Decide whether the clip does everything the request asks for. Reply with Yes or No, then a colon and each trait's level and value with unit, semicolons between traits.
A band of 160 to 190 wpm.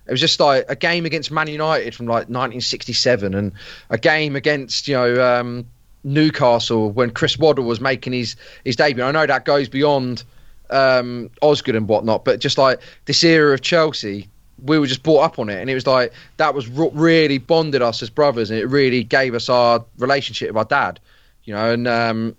No: fast, 205 wpm